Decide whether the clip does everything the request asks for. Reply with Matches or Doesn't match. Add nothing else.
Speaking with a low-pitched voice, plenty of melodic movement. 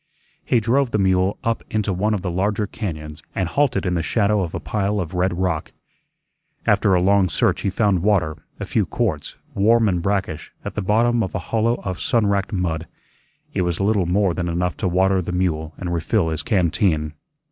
Doesn't match